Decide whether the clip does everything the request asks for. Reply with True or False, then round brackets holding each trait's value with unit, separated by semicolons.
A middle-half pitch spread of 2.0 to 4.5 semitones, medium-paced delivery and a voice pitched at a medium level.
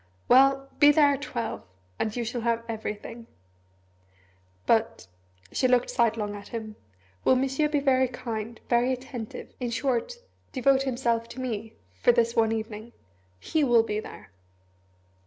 False (2.7 semitones; 145 wpm; 235 Hz)